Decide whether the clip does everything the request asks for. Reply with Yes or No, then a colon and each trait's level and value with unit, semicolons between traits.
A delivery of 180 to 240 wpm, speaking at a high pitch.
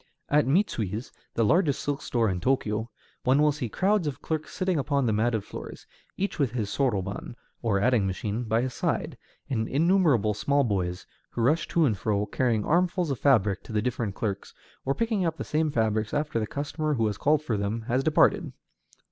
No: average, 195 wpm; low, 125 Hz